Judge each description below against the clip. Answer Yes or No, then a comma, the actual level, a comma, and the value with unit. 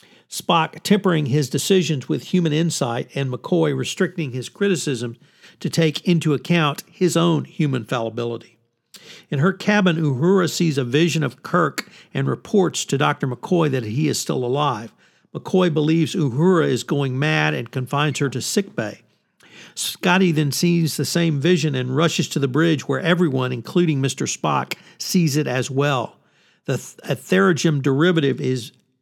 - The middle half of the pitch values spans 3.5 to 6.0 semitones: Yes, average, 4.1 semitones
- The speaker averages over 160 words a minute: No, average, 155 wpm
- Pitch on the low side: No, medium, 155 Hz